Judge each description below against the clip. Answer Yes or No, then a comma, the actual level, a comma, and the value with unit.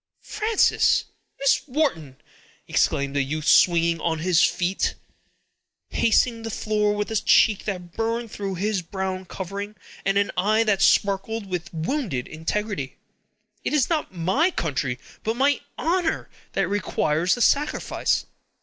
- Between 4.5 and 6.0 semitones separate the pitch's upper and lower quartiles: Yes, average, 4.9 semitones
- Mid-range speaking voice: No, high, 200 Hz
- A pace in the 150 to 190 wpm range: No, average, 140 wpm